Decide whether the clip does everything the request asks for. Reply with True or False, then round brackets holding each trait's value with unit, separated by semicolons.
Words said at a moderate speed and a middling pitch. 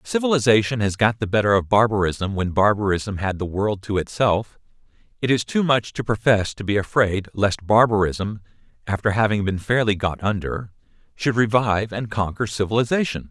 False (165 wpm; 105 Hz)